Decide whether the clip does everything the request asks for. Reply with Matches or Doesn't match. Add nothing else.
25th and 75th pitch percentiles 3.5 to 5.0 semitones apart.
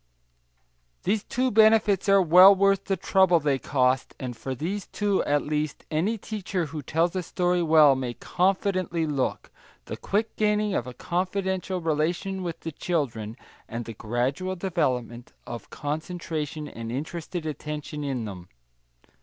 Doesn't match